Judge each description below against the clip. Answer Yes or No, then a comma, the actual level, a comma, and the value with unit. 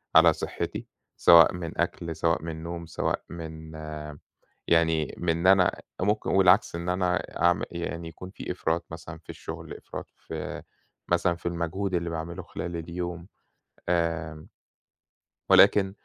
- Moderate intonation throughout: No, narrow, 1.3 semitones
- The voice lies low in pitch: Yes, very low, 85 Hz